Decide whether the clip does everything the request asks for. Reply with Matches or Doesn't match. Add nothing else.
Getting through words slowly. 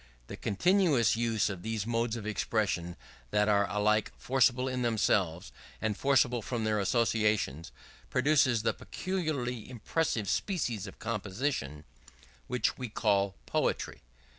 Matches